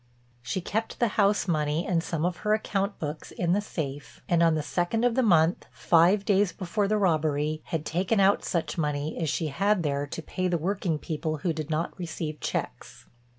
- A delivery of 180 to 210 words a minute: Yes, average, 195 wpm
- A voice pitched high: No, medium, 170 Hz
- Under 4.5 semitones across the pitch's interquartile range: Yes, average, 4.1 semitones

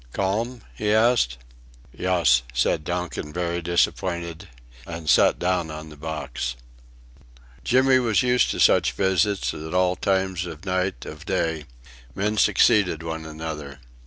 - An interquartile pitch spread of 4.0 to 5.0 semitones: No, average, 3.6 semitones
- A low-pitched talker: Yes, very low, 90 Hz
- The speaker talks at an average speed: No, slow, 130 wpm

